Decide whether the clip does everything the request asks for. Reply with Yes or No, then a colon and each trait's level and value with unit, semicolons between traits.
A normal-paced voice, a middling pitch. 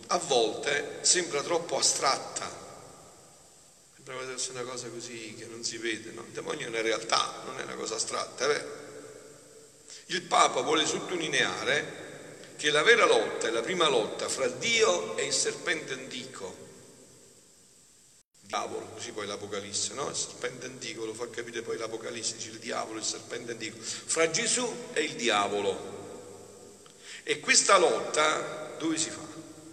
Yes: average, 150 wpm; medium, 160 Hz